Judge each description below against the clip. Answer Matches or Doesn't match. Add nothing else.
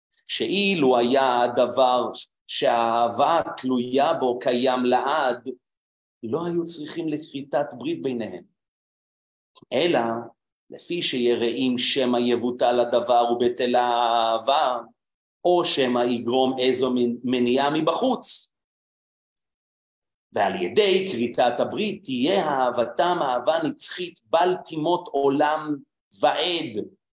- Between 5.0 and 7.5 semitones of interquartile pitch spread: Matches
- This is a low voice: Matches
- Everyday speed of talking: Doesn't match